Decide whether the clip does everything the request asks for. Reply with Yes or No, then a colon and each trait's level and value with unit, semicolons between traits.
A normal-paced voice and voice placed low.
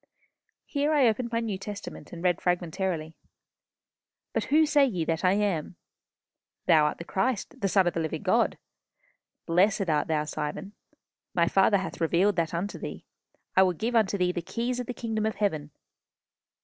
No: average, 175 wpm; high, 190 Hz